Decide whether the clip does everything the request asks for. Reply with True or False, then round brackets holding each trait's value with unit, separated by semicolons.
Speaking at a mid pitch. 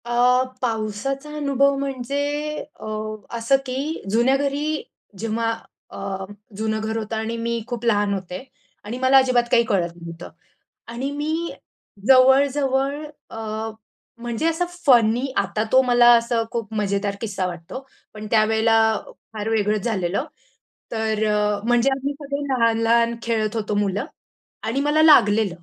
False (230 Hz)